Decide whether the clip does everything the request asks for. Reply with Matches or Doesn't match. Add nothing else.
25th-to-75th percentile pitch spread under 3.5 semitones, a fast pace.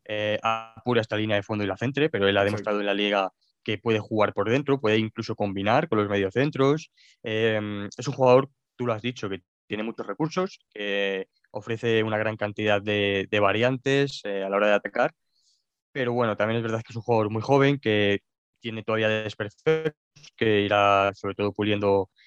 Matches